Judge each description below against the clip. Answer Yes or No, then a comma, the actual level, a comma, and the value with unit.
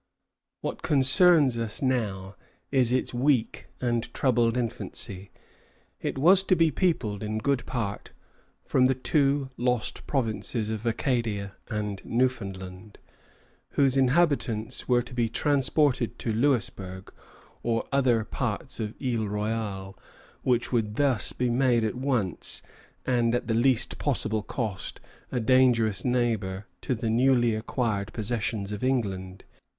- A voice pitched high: No, low, 120 Hz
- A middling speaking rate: No, slow, 130 wpm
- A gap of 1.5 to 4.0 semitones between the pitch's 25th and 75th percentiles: Yes, average, 3.4 semitones